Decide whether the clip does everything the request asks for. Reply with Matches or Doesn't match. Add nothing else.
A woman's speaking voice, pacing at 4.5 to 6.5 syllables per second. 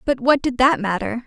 Matches